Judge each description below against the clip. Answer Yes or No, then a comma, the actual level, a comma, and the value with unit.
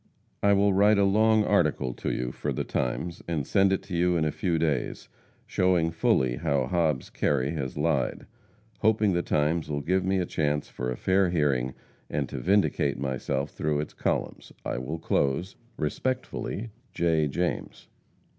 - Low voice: Yes, very low, 80 Hz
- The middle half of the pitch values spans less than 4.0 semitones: No, average, 5.0 semitones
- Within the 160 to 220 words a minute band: Yes, average, 170 wpm